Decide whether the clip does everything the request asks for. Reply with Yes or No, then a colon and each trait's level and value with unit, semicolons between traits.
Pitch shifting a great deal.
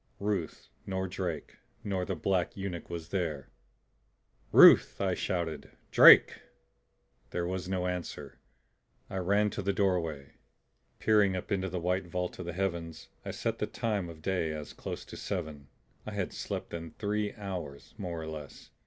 No: average, 2.7 semitones